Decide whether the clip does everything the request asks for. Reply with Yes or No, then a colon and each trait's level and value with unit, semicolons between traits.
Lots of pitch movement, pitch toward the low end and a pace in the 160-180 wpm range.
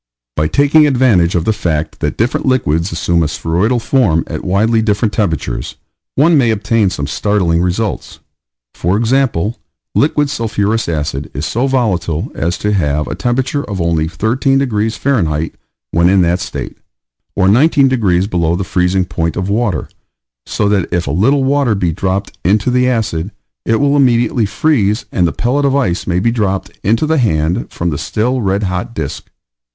Yes: wide, 6.0 semitones; low, 105 Hz; average, 175 wpm